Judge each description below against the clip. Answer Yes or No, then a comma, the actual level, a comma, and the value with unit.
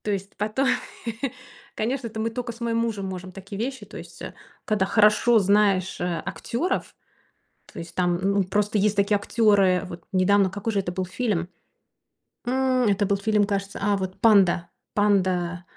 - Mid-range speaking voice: No, high, 200 Hz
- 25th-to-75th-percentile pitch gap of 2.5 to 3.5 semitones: Yes, average, 2.8 semitones